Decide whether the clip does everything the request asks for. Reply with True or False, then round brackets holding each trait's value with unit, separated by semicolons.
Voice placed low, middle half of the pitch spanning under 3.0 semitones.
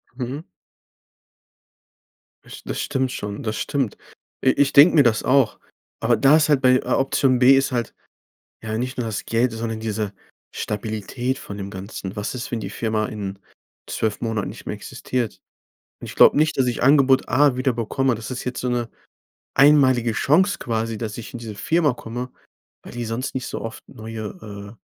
False (120 Hz; 3.3 semitones)